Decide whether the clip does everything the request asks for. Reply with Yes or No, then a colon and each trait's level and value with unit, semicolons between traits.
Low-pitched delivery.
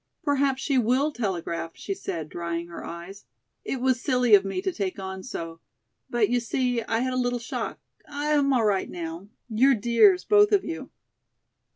No: high, 240 Hz